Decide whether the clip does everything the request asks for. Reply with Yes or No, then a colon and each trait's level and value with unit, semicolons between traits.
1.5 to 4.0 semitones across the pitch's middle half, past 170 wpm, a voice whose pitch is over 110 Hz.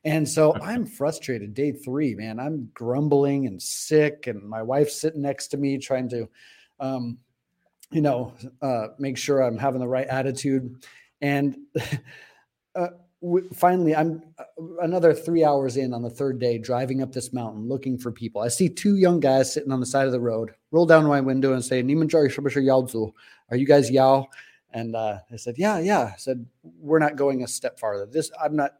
Yes: average, 3.4 semitones; average, 185 wpm; low, 135 Hz